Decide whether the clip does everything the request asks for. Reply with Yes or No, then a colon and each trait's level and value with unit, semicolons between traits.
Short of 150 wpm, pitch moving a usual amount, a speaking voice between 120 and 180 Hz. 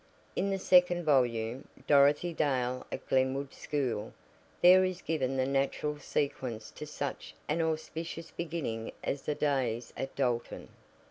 Yes: slow, 135 wpm; average, 3.9 semitones; medium, 140 Hz